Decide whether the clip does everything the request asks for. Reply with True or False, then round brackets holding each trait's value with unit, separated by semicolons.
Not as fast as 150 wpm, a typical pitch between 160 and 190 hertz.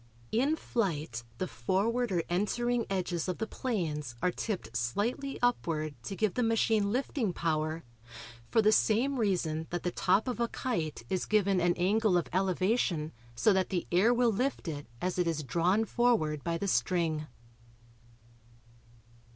False (160 wpm; 185 Hz)